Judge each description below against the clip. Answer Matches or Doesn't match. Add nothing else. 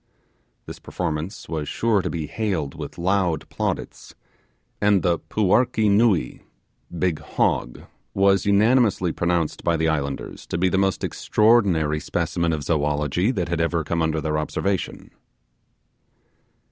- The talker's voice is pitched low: Matches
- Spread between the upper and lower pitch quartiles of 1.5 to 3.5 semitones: Doesn't match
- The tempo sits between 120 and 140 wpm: Matches